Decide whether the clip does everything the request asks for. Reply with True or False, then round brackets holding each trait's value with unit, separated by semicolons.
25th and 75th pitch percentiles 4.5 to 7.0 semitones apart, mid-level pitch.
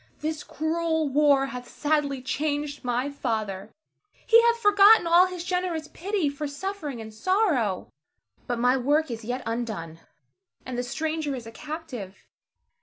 False (5.0 semitones; 290 Hz)